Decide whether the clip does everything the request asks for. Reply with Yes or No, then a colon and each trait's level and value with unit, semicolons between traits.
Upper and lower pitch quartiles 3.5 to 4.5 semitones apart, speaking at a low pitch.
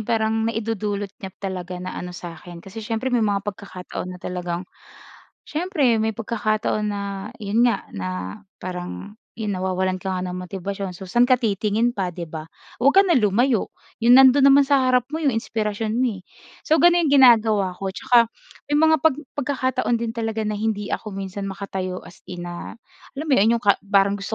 No: average, 4.1 semitones; high, 210 Hz